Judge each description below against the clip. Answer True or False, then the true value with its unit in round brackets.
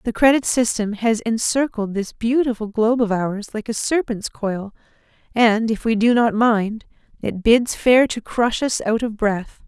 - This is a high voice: True (225 Hz)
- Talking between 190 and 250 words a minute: False (180 wpm)